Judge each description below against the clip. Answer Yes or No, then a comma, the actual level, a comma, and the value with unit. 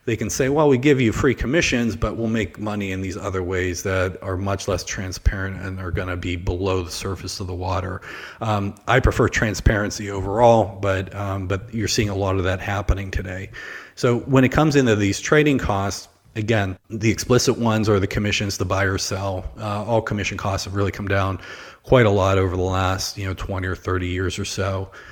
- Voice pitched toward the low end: Yes, low, 100 Hz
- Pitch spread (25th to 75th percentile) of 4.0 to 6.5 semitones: No, average, 2.7 semitones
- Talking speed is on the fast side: Yes, fast, 215 wpm